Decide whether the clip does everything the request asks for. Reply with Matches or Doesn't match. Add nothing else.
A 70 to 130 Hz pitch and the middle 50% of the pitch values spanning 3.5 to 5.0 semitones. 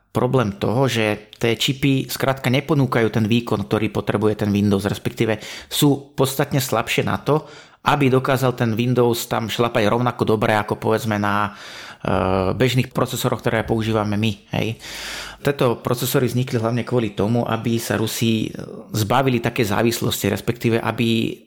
Doesn't match